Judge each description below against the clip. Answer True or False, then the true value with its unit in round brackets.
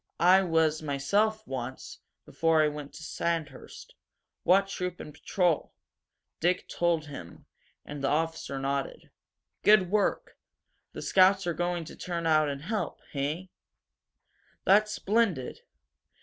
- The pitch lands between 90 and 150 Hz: False (165 Hz)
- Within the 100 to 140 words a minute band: True (135 wpm)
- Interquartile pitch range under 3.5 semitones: False (4.2 semitones)